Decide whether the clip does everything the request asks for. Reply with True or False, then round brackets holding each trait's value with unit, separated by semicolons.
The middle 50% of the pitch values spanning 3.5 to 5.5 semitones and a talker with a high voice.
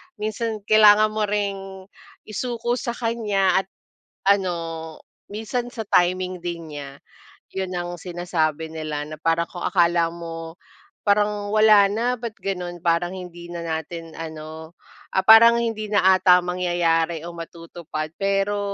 False (3.8 semitones; 180 Hz)